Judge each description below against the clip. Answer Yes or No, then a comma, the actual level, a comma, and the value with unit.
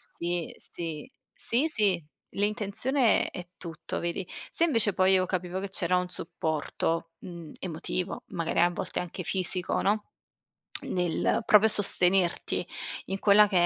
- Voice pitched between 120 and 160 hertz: No, medium, 185 Hz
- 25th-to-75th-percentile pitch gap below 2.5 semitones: No, average, 2.9 semitones